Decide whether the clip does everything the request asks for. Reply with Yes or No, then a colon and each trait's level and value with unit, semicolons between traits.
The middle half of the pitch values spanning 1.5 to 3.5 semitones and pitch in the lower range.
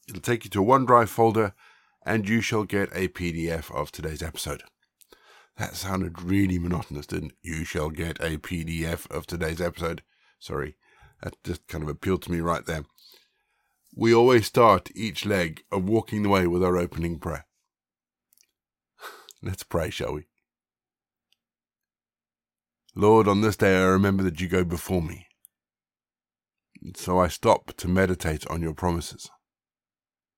Yes: average, 3.1 semitones; very low, 90 Hz